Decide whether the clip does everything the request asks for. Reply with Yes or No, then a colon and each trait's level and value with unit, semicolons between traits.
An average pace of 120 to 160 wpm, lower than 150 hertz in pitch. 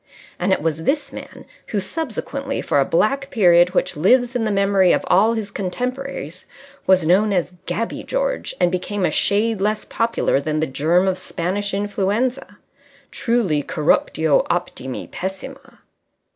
No: average, 150 wpm; high, 195 Hz